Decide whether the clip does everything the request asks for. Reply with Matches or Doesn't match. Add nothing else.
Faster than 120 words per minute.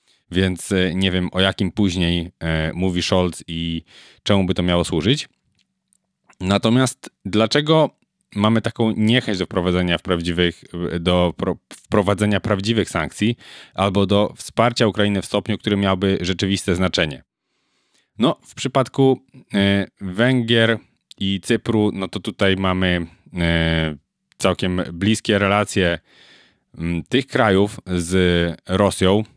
Doesn't match